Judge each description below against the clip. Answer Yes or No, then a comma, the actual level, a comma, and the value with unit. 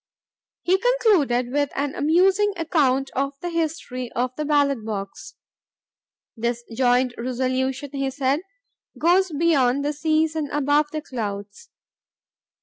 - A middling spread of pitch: Yes, average, 3.8 semitones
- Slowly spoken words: Yes, slow, 125 wpm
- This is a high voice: Yes, very high, 280 Hz